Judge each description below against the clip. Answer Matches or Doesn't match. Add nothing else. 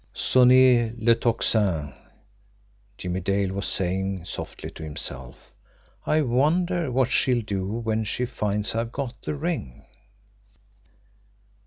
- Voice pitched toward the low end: Matches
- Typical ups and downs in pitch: Matches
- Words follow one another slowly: Matches